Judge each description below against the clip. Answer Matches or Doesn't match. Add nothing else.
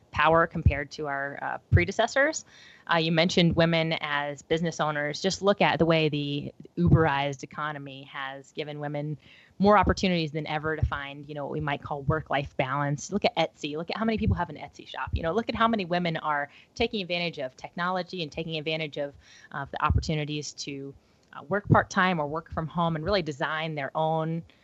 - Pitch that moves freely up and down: Doesn't match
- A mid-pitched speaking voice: Matches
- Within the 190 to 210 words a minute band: Matches